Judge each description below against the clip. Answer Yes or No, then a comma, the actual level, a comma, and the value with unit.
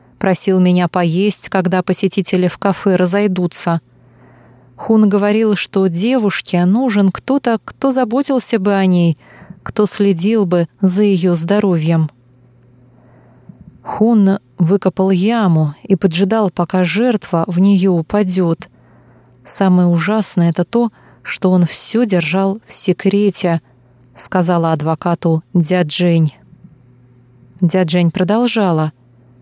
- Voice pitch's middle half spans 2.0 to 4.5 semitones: Yes, average, 3.5 semitones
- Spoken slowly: Yes, slow, 100 wpm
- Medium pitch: Yes, medium, 180 Hz